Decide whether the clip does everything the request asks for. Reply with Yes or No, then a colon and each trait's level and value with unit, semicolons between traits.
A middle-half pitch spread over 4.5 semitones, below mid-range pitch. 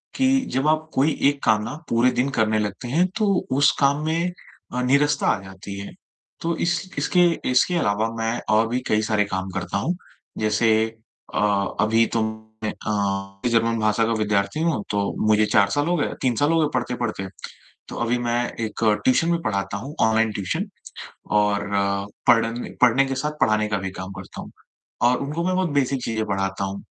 Yes: wide, 5.4 semitones; low, 115 Hz